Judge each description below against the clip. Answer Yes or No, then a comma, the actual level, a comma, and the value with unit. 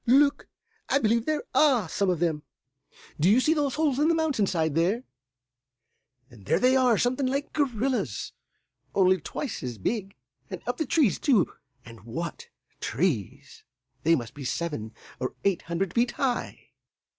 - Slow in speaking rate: No, average, 160 wpm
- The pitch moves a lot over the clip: Yes, wide, 8.4 semitones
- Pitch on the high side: Yes, high, 205 Hz